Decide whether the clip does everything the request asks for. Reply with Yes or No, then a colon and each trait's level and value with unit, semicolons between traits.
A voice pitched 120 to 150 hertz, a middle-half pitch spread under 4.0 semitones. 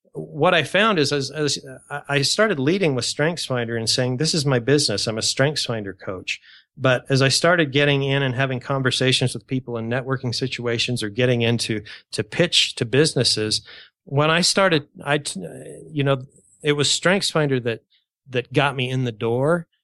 Yes: low, 135 Hz; average, 3.3 semitones